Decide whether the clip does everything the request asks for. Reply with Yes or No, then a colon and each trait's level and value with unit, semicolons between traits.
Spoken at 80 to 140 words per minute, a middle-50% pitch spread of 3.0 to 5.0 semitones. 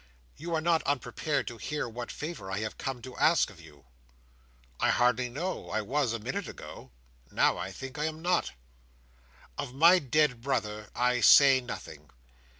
No: average, 170 wpm; average, 4.0 semitones